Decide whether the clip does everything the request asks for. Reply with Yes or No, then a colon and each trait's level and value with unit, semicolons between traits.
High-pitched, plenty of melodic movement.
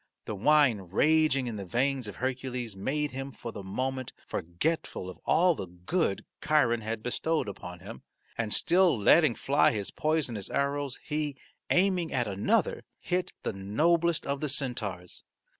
No: low, 130 Hz; wide, 6.7 semitones